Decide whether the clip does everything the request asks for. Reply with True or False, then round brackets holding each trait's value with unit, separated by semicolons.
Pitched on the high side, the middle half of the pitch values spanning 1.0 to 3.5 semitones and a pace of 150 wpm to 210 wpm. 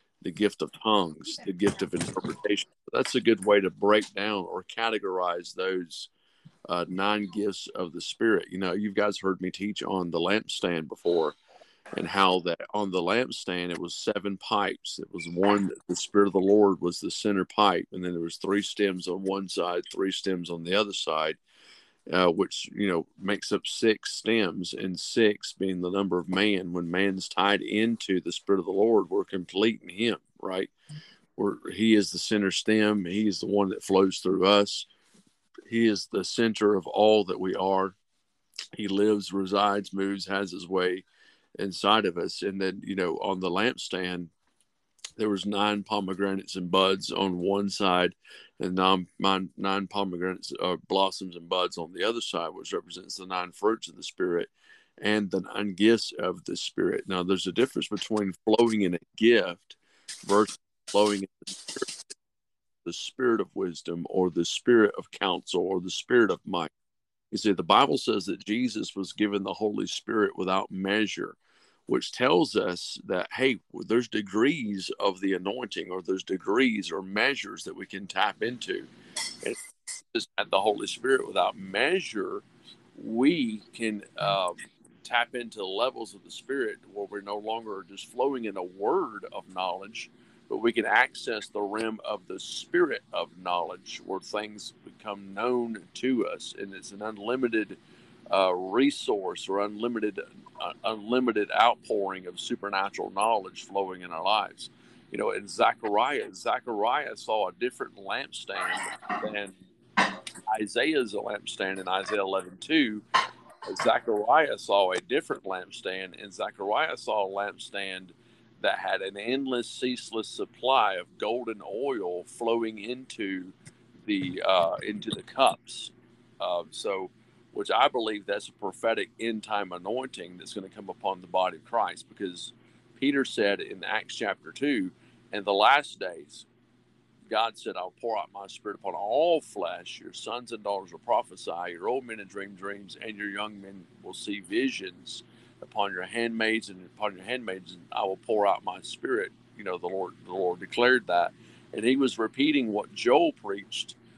False (100 Hz; 2.8 semitones; 170 wpm)